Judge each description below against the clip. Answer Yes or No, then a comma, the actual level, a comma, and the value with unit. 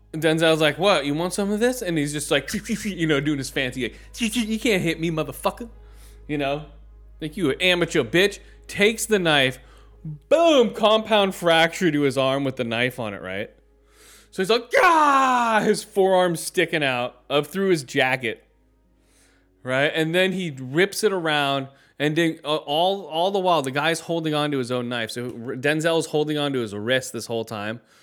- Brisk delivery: No, average, 185 wpm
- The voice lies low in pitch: No, medium, 155 Hz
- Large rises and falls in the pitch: Yes, wide, 6.2 semitones